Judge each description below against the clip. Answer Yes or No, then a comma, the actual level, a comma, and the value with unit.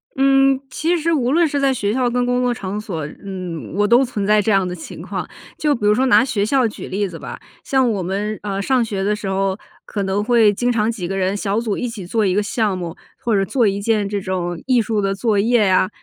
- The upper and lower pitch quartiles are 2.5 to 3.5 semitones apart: No, average, 4.0 semitones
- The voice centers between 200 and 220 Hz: Yes, high, 210 Hz